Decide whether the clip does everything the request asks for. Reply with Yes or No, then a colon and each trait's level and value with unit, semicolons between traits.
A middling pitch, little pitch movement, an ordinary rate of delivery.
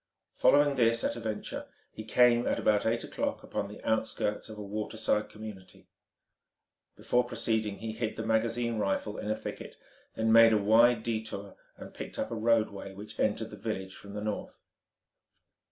No: low, 110 Hz; narrow, 1.5 semitones; average, 170 wpm